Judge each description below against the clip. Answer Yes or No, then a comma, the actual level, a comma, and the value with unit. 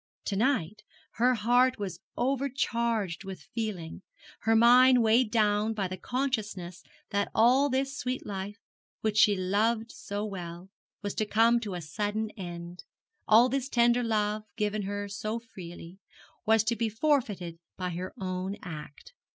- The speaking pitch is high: Yes, high, 215 Hz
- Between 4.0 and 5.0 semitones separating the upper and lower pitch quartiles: No, average, 3.6 semitones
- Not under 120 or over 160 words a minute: Yes, average, 150 wpm